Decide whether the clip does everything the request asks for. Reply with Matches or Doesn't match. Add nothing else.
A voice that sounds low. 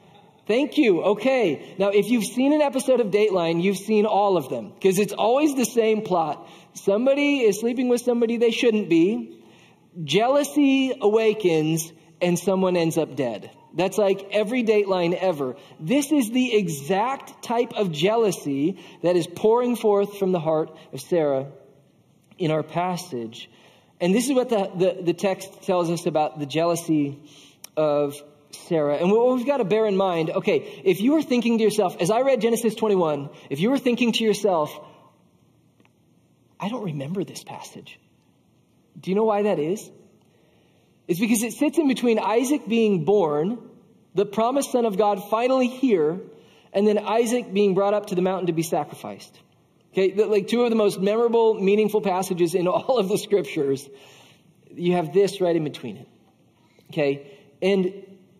Doesn't match